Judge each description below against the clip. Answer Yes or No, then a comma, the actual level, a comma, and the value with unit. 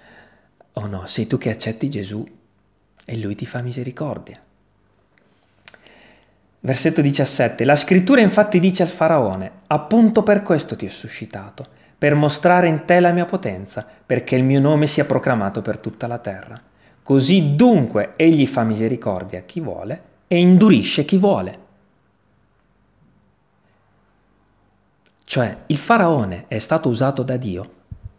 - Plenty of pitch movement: Yes, wide, 6.8 semitones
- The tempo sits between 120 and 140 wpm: Yes, average, 135 wpm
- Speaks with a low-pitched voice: Yes, low, 130 Hz